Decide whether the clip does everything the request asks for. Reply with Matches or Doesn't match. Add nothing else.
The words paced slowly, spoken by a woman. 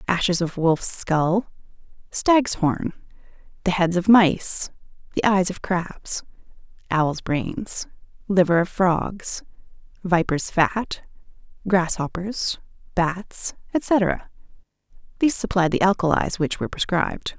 Matches